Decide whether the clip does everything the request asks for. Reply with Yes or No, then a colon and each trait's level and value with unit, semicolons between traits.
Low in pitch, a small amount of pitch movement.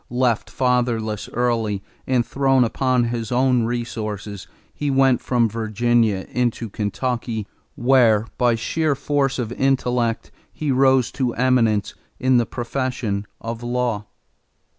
Yes: low, 120 Hz; narrow, 2.3 semitones